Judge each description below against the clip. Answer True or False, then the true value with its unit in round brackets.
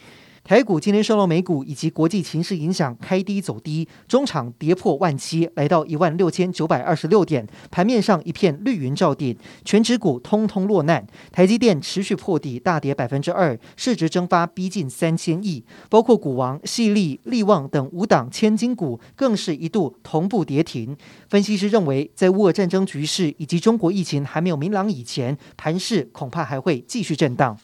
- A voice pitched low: False (175 Hz)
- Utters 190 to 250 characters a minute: False (290 characters per minute)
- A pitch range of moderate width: True (4.8 semitones)